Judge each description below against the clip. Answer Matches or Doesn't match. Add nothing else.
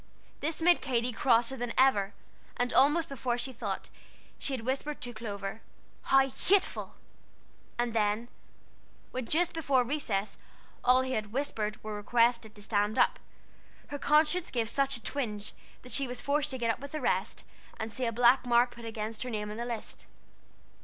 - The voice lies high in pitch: Matches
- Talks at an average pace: Matches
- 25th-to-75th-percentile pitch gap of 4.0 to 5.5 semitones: Doesn't match